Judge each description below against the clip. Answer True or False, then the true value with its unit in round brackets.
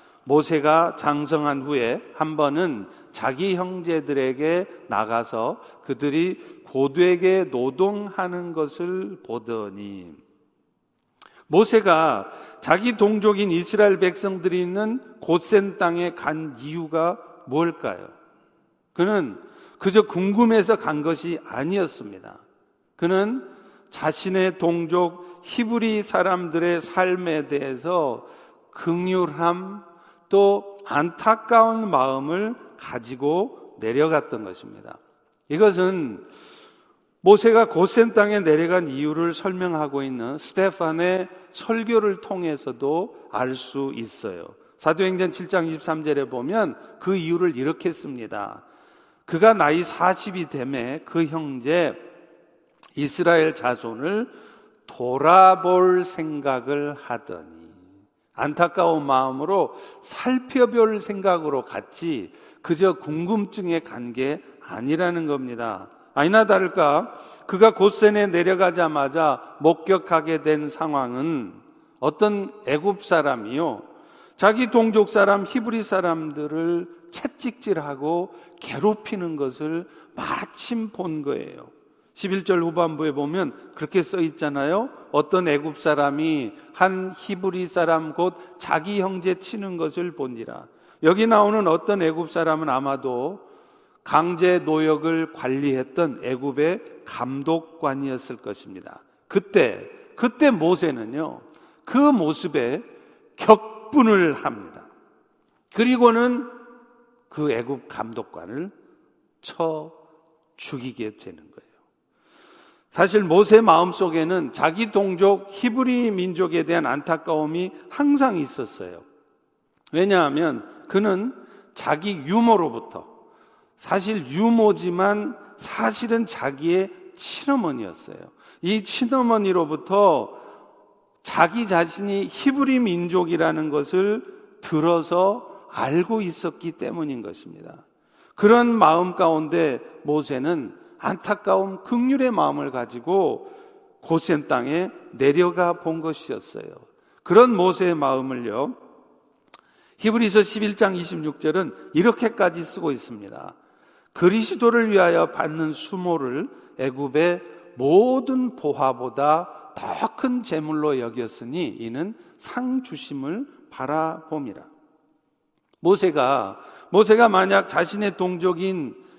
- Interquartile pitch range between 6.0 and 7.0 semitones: False (5.6 semitones)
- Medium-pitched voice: True (180 Hz)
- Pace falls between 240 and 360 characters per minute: False (225 characters per minute)